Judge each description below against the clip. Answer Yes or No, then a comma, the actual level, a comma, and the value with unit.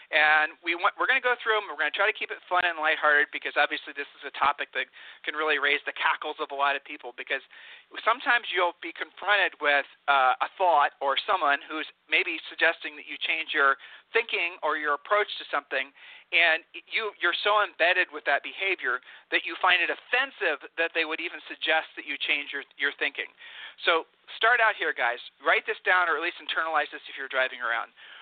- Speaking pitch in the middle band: Yes, medium, 170 Hz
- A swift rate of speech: Yes, fast, 215 wpm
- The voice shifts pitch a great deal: Yes, wide, 6.4 semitones